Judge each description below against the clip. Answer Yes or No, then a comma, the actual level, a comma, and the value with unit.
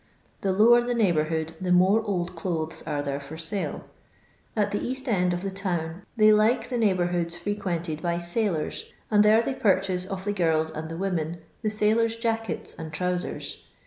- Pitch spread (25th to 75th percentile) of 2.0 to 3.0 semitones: No, average, 4.2 semitones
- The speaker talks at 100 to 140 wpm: No, average, 175 wpm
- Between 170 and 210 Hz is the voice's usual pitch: Yes, medium, 185 Hz